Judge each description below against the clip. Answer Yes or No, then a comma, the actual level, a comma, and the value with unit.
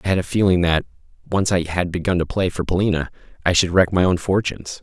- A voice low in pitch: Yes, very low, 90 Hz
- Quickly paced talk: Yes, fast, 235 wpm